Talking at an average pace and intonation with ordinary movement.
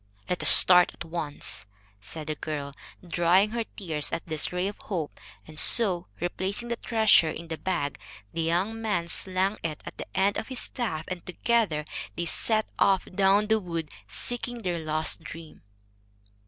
Yes: average, 170 wpm; average, 4.5 semitones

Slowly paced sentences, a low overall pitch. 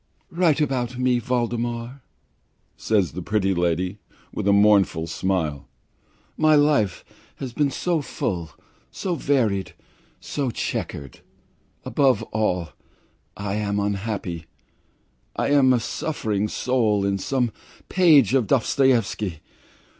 Yes: slow, 110 wpm; low, 110 Hz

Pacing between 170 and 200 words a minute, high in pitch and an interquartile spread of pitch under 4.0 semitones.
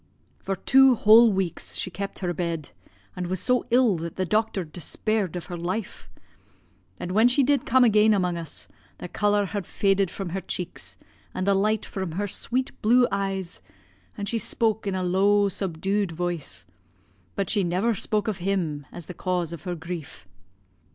Yes: average, 180 wpm; high, 195 Hz; average, 3.3 semitones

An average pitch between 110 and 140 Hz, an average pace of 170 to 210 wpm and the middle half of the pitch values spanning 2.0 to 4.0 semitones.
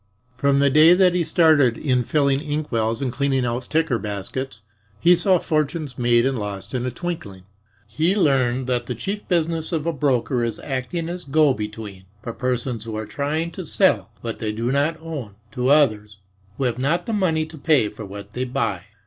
No: low, 135 Hz; average, 195 wpm; average, 5.2 semitones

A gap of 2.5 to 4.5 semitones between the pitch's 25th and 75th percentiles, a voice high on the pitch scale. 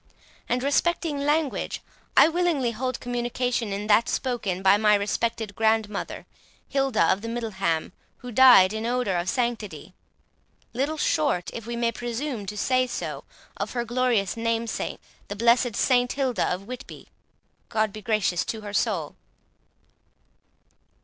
Yes: average, 3.3 semitones; high, 230 Hz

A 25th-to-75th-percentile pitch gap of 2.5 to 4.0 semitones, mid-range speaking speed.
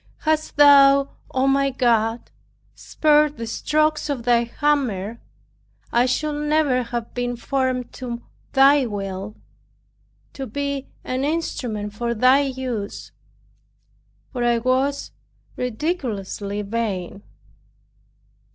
No: average, 3.4 semitones; slow, 105 wpm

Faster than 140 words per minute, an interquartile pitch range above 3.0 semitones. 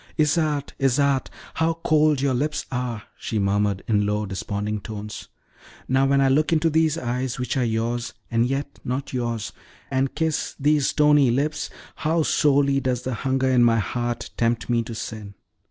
Yes: average, 170 wpm; average, 4.0 semitones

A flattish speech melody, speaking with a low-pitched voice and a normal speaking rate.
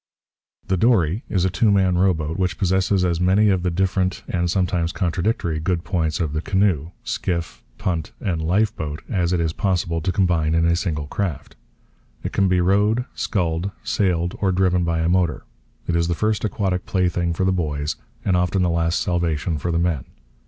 Yes: narrow, 2.3 semitones; very low, 90 Hz; average, 190 wpm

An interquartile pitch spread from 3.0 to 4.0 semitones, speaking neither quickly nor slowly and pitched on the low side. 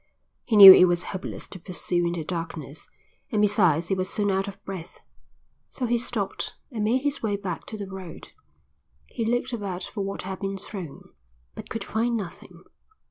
No: average, 3.4 semitones; average, 190 wpm; high, 195 Hz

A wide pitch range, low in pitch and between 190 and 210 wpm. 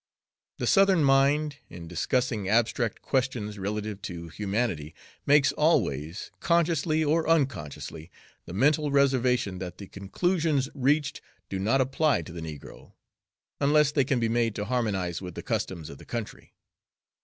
No: wide, 7.1 semitones; low, 120 Hz; average, 145 wpm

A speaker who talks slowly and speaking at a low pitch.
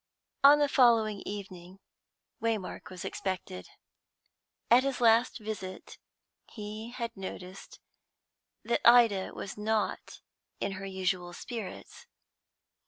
No: slow, 105 wpm; high, 210 Hz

